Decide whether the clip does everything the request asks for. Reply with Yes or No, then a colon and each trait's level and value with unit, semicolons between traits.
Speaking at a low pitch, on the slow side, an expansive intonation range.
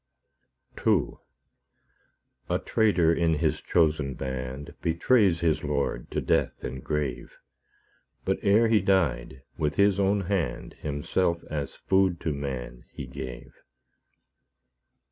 Yes: very low, 80 Hz; slow, 115 wpm; wide, 6.0 semitones